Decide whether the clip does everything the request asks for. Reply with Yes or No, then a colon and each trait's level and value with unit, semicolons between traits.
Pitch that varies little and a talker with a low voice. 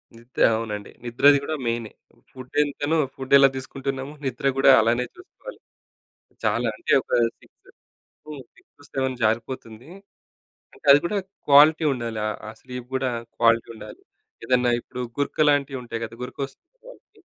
No: average, 3.3 semitones; low, 130 Hz